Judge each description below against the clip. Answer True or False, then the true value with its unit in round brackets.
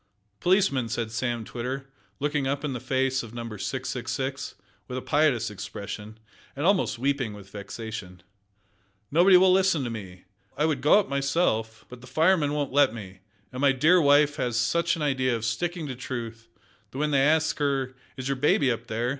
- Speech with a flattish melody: False (4.4 semitones)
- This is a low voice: True (130 Hz)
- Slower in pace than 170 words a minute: False (185 wpm)